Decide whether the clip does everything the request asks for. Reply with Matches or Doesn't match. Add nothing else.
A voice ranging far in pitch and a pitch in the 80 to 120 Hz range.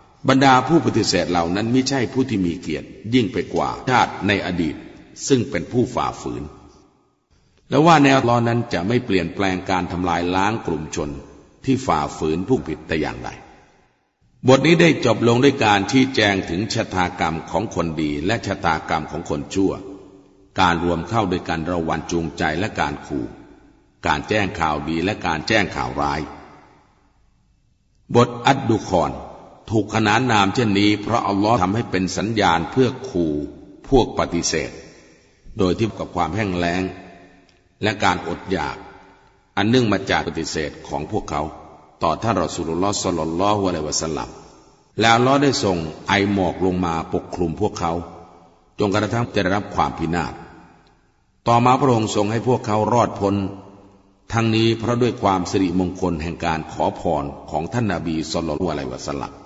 Doesn't match